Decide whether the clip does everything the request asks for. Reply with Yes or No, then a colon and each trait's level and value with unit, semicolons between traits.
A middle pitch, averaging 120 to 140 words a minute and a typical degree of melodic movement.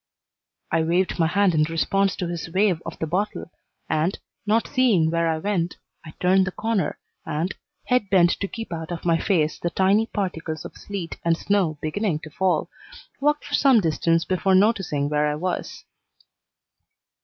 No: medium, 180 Hz; average, 175 wpm; average, 3.6 semitones